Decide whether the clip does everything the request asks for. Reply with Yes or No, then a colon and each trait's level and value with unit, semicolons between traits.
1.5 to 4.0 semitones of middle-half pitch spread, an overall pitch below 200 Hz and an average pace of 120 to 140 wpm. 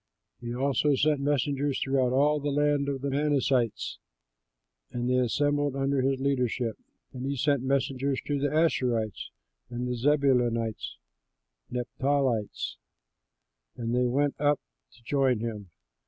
Yes: narrow, 2.6 semitones; low, 135 Hz; slow, 135 wpm